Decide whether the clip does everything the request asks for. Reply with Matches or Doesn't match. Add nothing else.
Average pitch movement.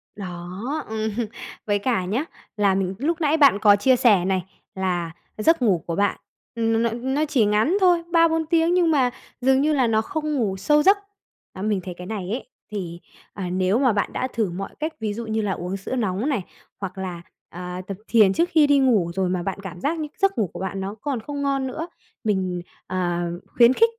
Doesn't match